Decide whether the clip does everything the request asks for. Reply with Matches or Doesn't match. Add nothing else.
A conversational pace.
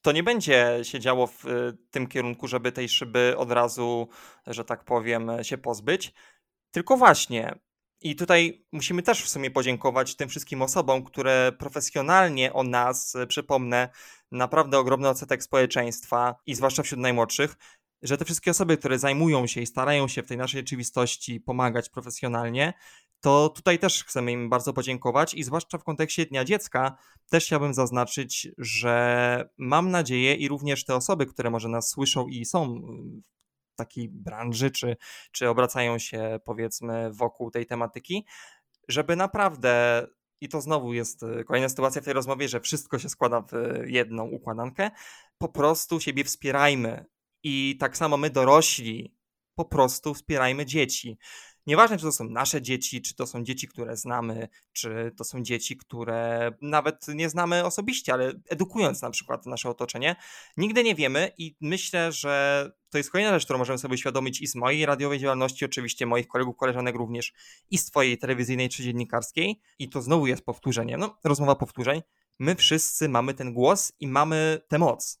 Doesn't match